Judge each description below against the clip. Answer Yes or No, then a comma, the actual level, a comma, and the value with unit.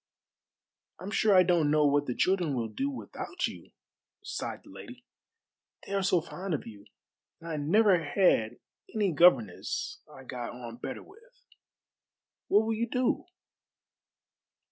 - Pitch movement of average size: No, wide, 7.5 semitones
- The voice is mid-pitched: Yes, medium, 180 Hz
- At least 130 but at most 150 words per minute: Yes, average, 145 wpm